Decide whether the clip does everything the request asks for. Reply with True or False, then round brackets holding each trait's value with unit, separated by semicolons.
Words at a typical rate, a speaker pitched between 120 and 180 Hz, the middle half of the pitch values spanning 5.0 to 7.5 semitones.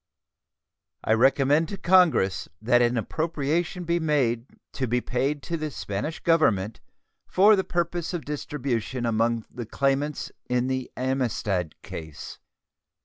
False (130 wpm; 135 Hz; 5.3 semitones)